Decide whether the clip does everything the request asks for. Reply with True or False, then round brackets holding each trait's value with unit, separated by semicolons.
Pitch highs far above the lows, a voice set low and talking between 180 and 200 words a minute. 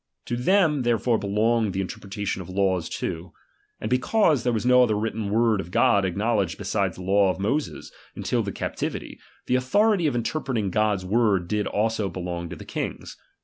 False (3.9 semitones; 105 Hz; 185 wpm)